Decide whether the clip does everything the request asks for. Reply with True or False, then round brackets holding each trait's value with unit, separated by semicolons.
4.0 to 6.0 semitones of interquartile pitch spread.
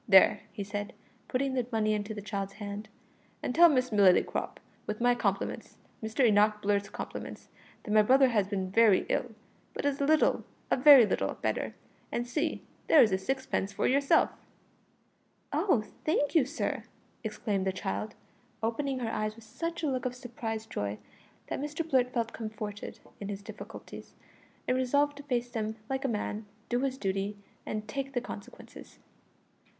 True (4.4 semitones)